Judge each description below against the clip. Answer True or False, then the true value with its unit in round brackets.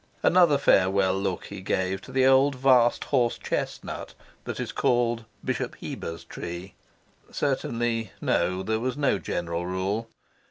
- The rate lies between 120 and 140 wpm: True (135 wpm)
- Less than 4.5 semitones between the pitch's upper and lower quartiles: False (5.6 semitones)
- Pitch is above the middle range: False (115 Hz)